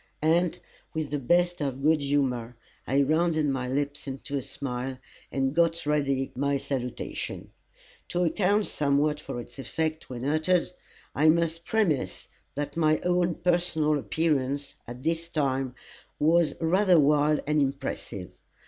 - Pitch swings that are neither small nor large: Yes, average, 3.4 semitones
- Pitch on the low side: No, medium, 150 Hz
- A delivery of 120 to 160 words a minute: Yes, average, 140 wpm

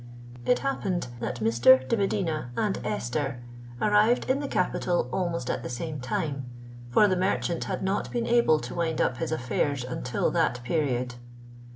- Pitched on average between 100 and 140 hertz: No, medium, 155 Hz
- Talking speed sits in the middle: Yes, average, 165 wpm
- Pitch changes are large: Yes, wide, 7.5 semitones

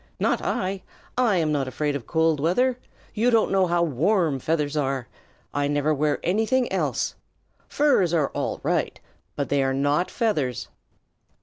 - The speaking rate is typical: Yes, average, 150 wpm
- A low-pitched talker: No, medium, 160 Hz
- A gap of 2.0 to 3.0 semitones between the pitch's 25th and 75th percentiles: No, wide, 5.4 semitones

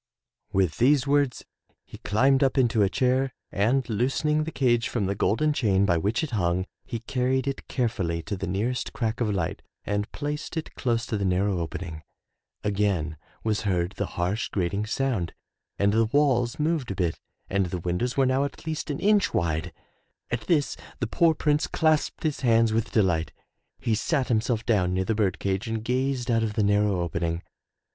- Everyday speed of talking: Yes, average, 190 wpm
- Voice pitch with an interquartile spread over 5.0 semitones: Yes, wide, 5.4 semitones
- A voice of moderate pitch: No, low, 110 Hz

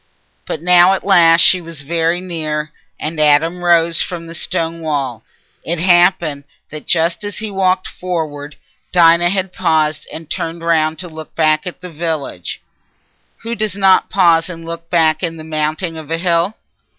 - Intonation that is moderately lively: No, narrow, 2.1 semitones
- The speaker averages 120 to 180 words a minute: Yes, average, 160 wpm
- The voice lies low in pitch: No, medium, 165 Hz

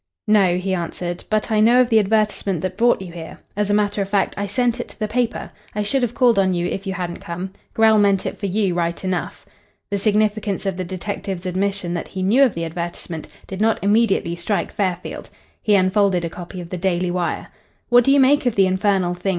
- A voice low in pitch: No, high, 195 Hz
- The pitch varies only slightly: No, average, 3.1 semitones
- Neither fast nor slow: No, fast, 230 wpm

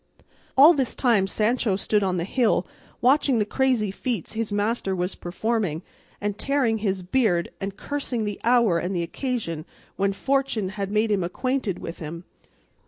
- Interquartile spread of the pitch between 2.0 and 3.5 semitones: No, average, 4.5 semitones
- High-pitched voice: Yes, high, 210 Hz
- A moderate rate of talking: Yes, average, 165 wpm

